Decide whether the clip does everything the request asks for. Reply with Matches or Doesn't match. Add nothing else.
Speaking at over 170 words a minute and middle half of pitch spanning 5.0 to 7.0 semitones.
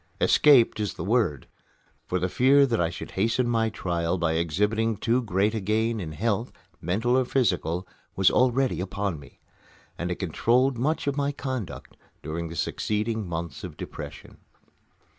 Doesn't match